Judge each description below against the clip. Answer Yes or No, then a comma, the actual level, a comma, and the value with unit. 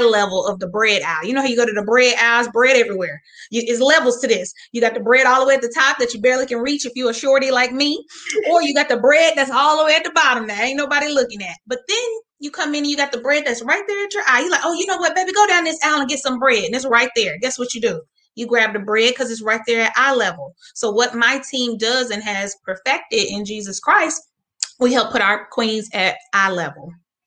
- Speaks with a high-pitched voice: Yes, very high, 250 Hz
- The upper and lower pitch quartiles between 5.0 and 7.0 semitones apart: No, average, 4.3 semitones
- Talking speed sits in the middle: No, fast, 285 wpm